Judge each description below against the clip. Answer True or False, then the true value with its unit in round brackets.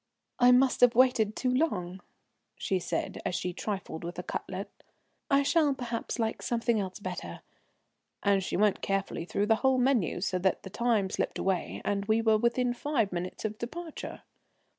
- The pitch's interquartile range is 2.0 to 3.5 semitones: False (4.5 semitones)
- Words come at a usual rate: True (175 wpm)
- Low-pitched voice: False (220 Hz)